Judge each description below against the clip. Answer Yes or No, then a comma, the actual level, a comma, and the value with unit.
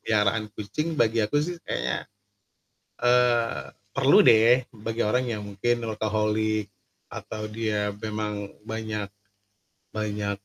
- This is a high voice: No, low, 110 Hz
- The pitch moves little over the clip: Yes, narrow, 1.7 semitones